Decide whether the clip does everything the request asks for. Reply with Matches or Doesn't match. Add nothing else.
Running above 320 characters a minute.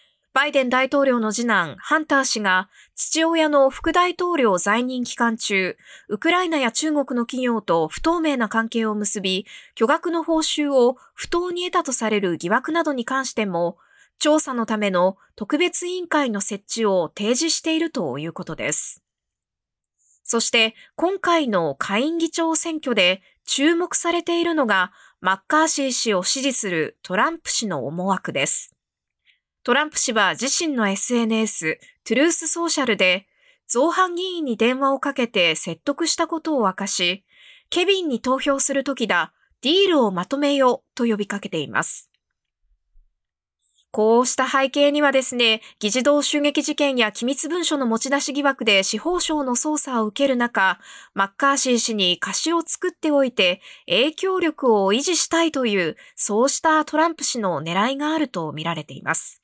Doesn't match